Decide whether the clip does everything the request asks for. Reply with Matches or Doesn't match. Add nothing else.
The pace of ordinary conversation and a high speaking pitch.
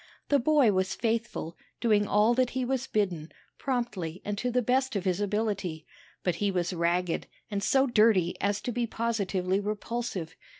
Matches